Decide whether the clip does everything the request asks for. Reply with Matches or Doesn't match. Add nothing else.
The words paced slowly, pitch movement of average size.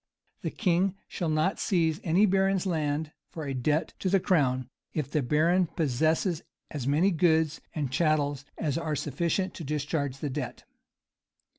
Doesn't match